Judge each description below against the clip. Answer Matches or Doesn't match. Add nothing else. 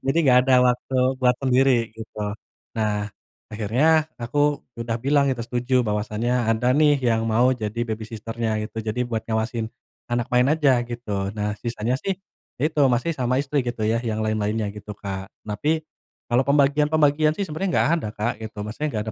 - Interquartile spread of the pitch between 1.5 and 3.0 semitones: Doesn't match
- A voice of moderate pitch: Doesn't match